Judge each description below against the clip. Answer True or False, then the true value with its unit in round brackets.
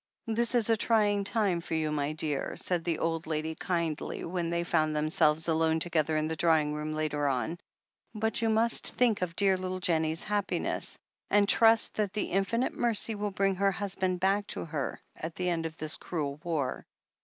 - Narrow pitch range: False (4.4 semitones)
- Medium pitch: True (170 Hz)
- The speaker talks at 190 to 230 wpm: True (195 wpm)